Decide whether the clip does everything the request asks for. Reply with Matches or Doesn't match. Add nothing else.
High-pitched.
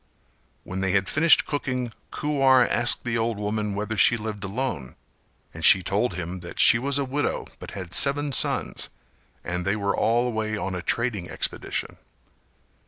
Doesn't match